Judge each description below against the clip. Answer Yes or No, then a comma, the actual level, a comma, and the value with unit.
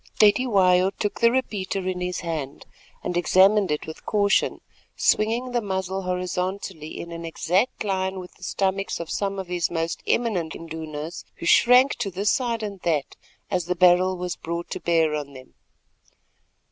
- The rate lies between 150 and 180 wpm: Yes, average, 165 wpm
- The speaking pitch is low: No, medium, 185 Hz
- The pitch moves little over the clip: No, average, 3.0 semitones